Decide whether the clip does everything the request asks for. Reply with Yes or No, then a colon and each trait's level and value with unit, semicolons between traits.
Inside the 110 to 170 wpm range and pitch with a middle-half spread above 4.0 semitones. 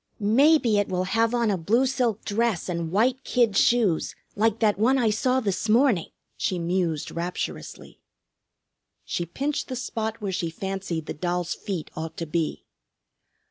Yes: average, 160 wpm; average, 5.2 semitones